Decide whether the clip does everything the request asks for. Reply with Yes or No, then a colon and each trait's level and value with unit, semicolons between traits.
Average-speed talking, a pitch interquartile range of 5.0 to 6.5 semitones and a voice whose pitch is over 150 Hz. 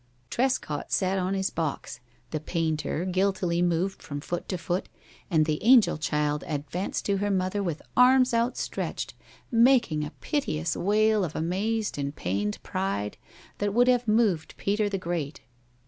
Yes: average, 150 wpm; average, 5.3 semitones; medium, 185 Hz